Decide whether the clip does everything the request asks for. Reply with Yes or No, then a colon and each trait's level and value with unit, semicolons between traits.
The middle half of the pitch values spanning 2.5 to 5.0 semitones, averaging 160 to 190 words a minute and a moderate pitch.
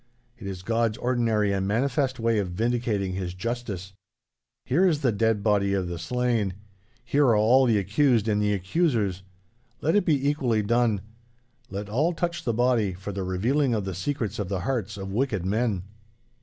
No: average, 4.2 semitones; average, 180 wpm; low, 110 Hz